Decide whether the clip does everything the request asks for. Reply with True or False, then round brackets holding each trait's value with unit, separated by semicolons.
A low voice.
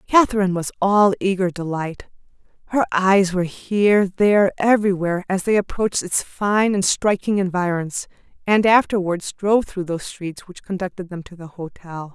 False (190 Hz)